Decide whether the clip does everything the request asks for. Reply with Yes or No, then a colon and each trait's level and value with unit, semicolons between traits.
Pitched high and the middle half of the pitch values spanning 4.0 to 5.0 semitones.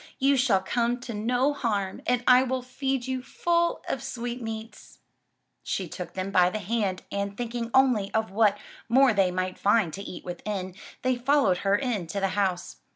Yes: high, 225 Hz; average, 4.5 semitones